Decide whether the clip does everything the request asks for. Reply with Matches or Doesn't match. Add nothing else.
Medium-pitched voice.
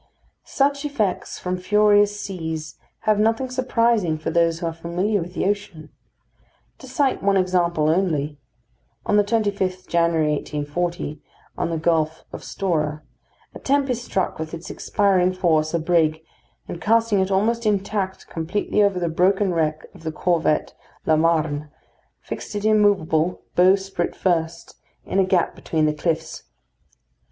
Matches